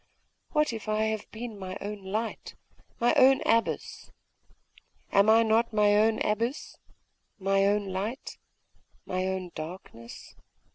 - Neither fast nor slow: No, slow, 130 wpm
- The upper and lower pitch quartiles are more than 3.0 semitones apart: No, average, 2.7 semitones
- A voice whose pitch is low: No, high, 210 Hz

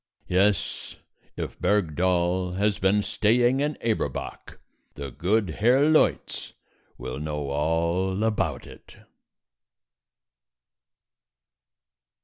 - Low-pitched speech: Yes, very low, 95 Hz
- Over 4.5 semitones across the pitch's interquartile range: Yes, average, 4.9 semitones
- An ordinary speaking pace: No, slow, 85 wpm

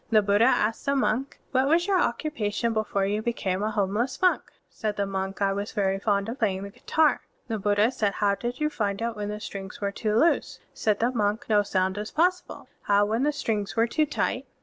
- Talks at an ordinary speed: No, fast, 220 wpm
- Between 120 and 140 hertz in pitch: No, high, 215 Hz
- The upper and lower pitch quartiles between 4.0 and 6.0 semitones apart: No, average, 3.3 semitones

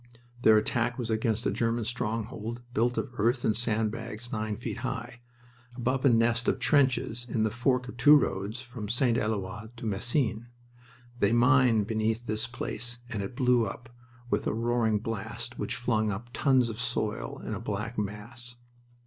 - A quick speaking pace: No, average, 175 wpm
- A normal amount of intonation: No, narrow, 2.0 semitones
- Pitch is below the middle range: Yes, low, 115 Hz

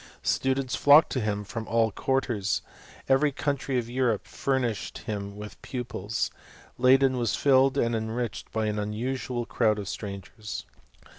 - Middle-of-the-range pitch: No, low, 120 Hz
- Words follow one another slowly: No, average, 145 wpm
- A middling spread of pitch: Yes, average, 3.7 semitones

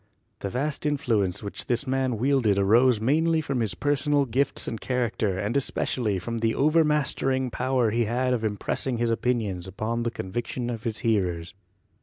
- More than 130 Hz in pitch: No, low, 120 Hz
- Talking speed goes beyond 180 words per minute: No, average, 170 wpm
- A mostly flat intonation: No, average, 3.6 semitones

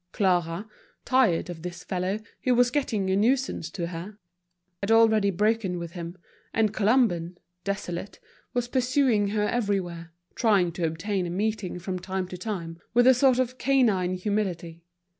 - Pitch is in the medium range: No, high, 200 Hz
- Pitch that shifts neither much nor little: Yes, average, 4.2 semitones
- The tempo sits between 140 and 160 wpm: Yes, average, 155 wpm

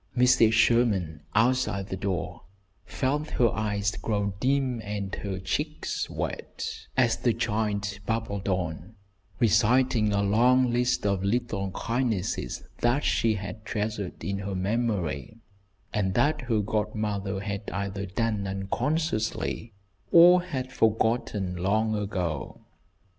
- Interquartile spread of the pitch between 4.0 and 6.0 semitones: No, average, 3.3 semitones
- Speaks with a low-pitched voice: Yes, low, 105 Hz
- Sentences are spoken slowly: Yes, slow, 120 wpm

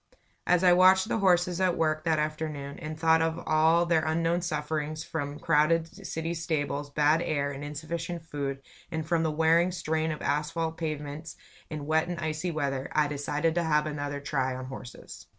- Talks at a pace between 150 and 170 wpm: No, average, 180 wpm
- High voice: No, medium, 155 Hz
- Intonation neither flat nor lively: No, narrow, 2.1 semitones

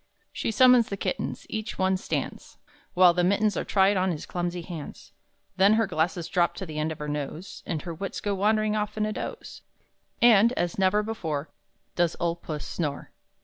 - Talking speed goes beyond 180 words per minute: Yes, average, 190 wpm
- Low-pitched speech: No, medium, 185 Hz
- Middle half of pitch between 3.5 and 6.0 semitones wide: Yes, average, 4.0 semitones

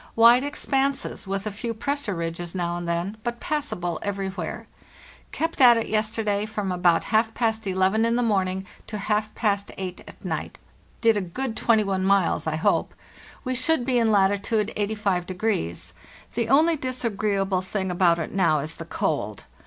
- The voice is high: Yes, high, 205 Hz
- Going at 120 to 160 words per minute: No, average, 170 wpm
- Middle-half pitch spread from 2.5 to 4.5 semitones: Yes, average, 3.7 semitones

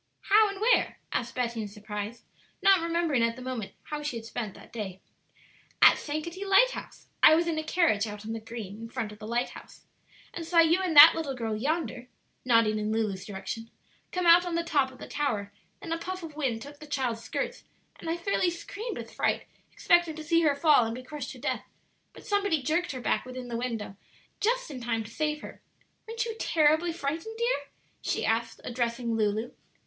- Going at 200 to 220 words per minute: Yes, fast, 205 wpm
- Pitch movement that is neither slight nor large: No, wide, 6.7 semitones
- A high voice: Yes, very high, 280 Hz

